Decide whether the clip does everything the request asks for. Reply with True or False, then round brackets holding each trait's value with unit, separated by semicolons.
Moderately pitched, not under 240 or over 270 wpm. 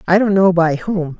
True (180 Hz; 250 wpm)